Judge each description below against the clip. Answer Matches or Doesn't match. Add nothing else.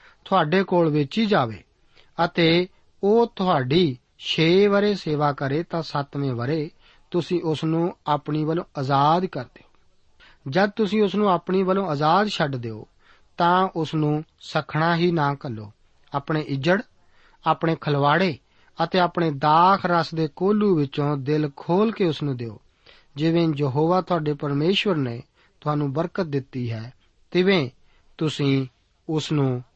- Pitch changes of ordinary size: Matches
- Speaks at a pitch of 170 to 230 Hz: Doesn't match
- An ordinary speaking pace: Matches